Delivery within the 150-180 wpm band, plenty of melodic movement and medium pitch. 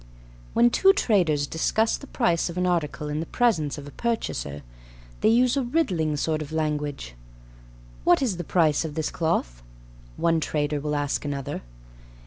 Yes: average, 165 wpm; wide, 6.8 semitones; medium, 160 Hz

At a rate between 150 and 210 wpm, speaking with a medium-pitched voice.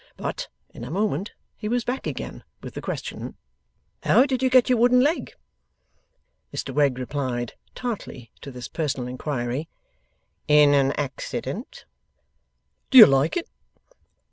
No: average, 140 wpm; medium, 150 Hz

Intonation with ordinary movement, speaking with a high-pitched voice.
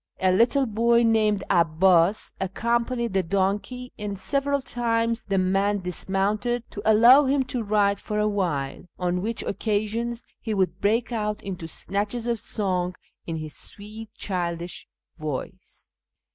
Yes: average, 3.7 semitones; high, 205 Hz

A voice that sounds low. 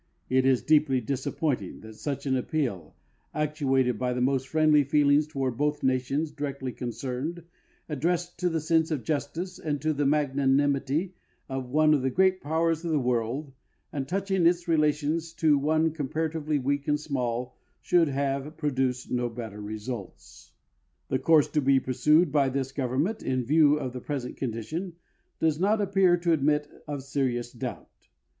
No: medium, 145 Hz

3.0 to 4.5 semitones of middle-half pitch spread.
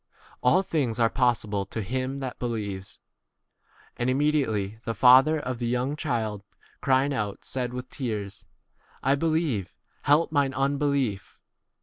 Yes: average, 4.2 semitones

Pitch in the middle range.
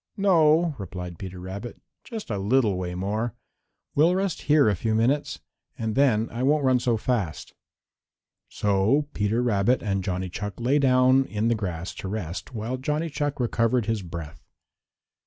No: low, 115 Hz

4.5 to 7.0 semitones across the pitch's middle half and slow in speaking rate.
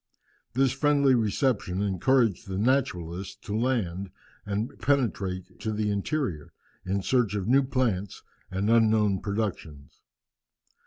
Yes: average, 5.1 semitones; slow, 115 wpm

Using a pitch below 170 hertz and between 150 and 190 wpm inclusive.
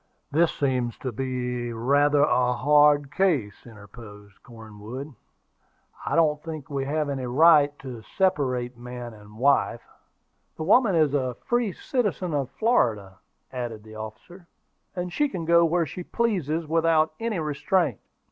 No: medium, 140 Hz; average, 140 wpm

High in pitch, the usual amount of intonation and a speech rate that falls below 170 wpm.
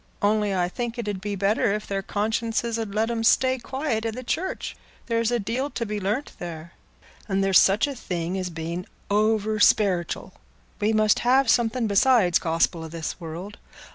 No: high, 210 Hz; average, 3.4 semitones; average, 175 wpm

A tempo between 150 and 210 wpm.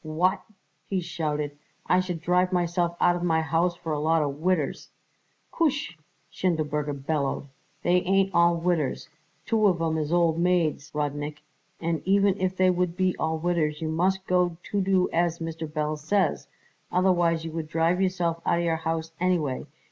Yes: average, 170 wpm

